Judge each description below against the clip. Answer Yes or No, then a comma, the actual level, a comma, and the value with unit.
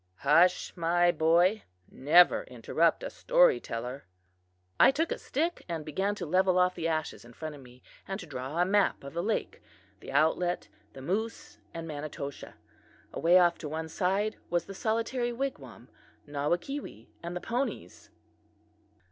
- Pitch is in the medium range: Yes, medium, 175 Hz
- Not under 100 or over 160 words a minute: Yes, average, 155 wpm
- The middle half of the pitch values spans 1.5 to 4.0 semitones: No, average, 5.2 semitones